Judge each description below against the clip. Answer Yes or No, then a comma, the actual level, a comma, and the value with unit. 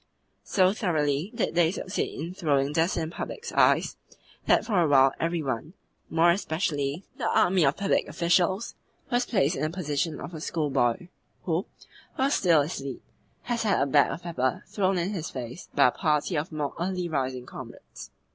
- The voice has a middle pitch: Yes, medium, 165 Hz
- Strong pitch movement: No, average, 4.2 semitones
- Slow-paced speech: No, average, 180 wpm